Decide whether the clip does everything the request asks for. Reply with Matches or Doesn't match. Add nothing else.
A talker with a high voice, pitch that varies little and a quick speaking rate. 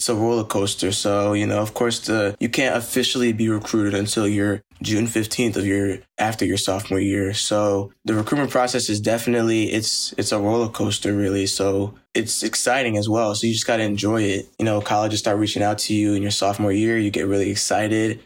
Doesn't match